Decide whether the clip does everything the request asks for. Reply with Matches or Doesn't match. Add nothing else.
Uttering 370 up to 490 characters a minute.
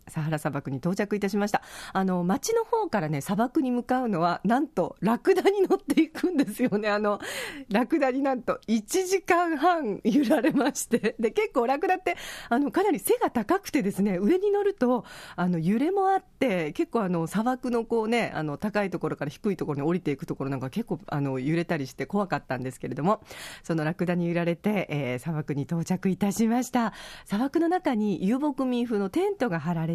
Matches